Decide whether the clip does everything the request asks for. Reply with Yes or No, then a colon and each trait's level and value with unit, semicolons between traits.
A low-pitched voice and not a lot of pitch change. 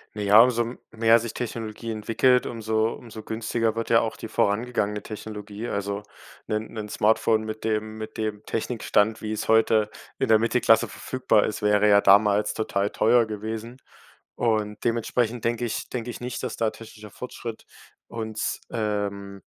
Yes: low, 110 Hz; narrow, 1.6 semitones